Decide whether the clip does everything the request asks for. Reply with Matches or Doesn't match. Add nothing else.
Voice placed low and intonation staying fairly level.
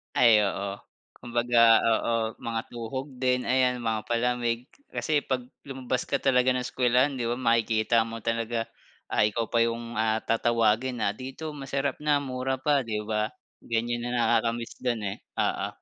Matches